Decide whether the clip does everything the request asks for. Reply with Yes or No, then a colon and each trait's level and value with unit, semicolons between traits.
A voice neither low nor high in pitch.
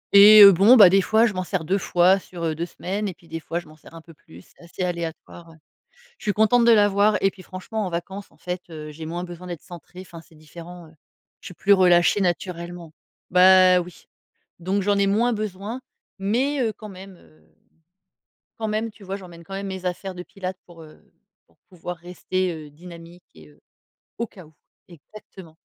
Yes: medium, 180 Hz